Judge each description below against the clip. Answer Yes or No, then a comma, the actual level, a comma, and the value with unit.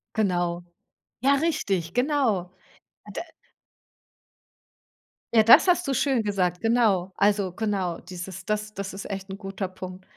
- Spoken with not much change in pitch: No, average, 3.6 semitones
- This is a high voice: Yes, high, 195 Hz